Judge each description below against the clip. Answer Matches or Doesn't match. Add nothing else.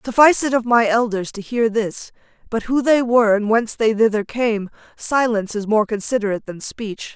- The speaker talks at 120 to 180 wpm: Doesn't match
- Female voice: Matches